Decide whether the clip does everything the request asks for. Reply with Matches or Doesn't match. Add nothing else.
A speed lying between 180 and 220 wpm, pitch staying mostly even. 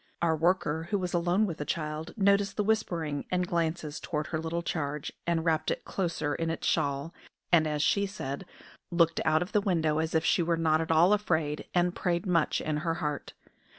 Matches